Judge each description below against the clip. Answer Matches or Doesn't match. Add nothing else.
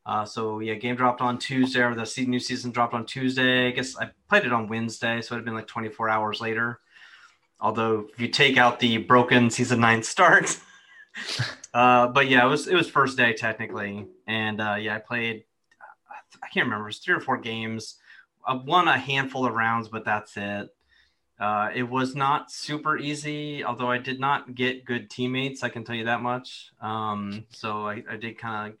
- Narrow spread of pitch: Matches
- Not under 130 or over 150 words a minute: Doesn't match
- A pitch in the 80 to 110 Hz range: Doesn't match